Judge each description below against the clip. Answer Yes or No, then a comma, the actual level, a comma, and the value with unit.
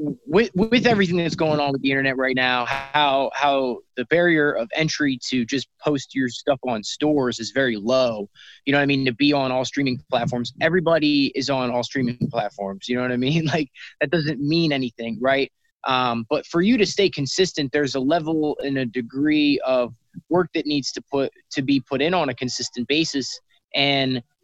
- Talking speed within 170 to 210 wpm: Yes, fast, 205 wpm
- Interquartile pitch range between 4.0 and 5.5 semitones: No, average, 3.4 semitones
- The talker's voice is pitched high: No, medium, 140 Hz